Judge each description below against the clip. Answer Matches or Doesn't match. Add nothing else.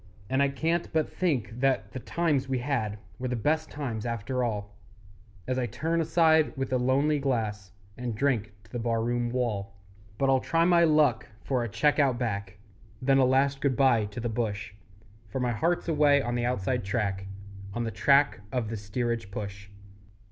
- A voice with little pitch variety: Doesn't match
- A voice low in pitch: Matches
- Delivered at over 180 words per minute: Matches